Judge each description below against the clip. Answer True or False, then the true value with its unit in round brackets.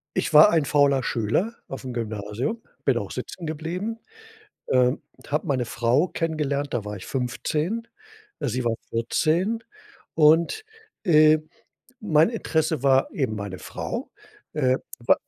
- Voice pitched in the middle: True (145 Hz)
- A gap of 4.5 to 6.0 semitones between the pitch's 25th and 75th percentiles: True (5.1 semitones)